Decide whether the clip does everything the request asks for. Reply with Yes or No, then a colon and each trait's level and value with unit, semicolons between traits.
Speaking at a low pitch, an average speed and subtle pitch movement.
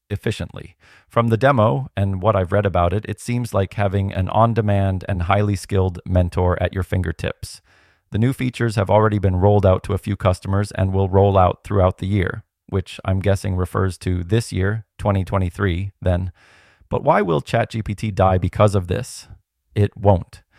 Yes: low, 100 Hz; average, 180 wpm; narrow, 2.3 semitones